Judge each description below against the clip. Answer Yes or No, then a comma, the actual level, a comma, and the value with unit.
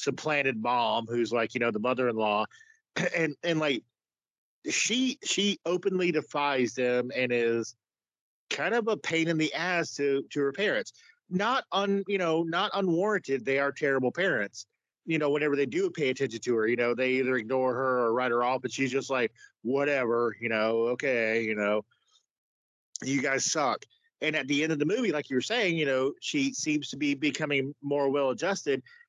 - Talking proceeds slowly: No, average, 190 wpm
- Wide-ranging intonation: Yes, wide, 5.9 semitones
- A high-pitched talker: No, medium, 140 Hz